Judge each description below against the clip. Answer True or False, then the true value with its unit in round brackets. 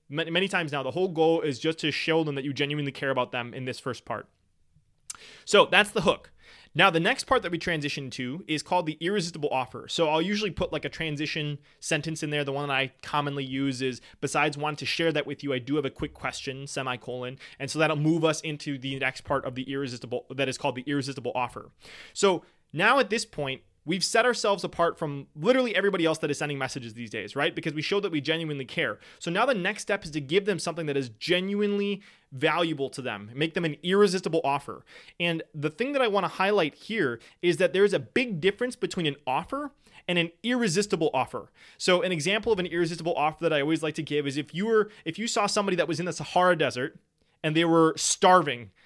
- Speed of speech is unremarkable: False (230 wpm)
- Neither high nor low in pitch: True (160 Hz)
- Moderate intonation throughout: True (4.5 semitones)